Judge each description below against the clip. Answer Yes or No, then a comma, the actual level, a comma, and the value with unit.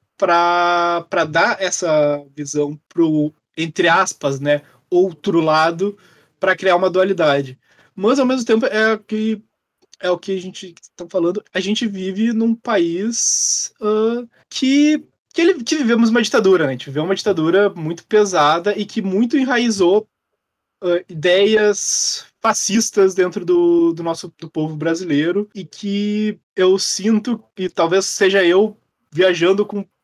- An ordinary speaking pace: Yes, average, 145 wpm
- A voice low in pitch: No, high, 190 Hz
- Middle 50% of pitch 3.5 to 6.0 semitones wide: Yes, average, 4.3 semitones